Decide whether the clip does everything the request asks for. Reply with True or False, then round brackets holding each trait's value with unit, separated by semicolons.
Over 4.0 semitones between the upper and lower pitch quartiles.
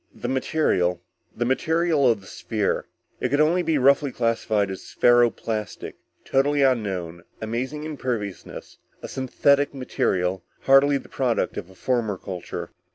True (5.6 semitones)